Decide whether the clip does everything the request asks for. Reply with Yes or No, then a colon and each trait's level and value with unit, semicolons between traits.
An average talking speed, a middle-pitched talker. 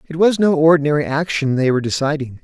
Yes: average, 195 wpm; medium, 150 Hz